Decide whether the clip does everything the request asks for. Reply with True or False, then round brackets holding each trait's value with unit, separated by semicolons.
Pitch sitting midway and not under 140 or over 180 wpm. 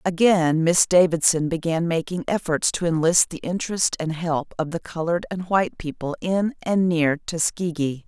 True (170 Hz; 165 wpm)